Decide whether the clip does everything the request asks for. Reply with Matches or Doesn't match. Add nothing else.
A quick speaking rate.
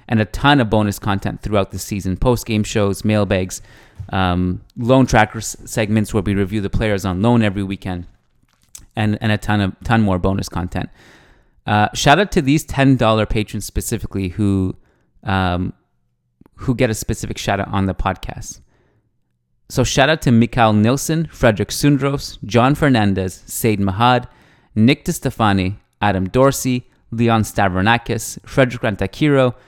Doesn't match